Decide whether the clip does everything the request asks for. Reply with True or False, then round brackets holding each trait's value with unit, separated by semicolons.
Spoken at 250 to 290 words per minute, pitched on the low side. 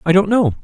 False (285 wpm; 185 Hz)